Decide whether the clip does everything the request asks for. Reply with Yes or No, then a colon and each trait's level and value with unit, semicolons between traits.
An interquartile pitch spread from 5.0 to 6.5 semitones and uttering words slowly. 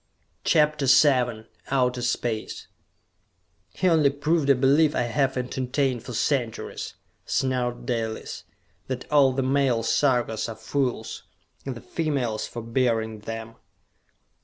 No: average, 3.2 semitones; slow, 120 wpm